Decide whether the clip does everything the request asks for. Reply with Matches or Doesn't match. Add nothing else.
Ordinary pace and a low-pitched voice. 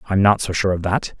Doesn't match